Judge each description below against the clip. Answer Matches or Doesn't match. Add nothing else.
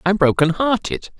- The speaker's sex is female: Doesn't match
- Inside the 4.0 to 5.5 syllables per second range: Doesn't match